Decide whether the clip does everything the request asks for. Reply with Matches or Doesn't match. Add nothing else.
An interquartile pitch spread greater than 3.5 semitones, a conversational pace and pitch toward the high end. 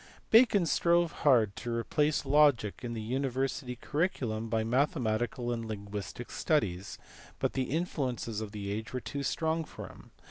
Doesn't match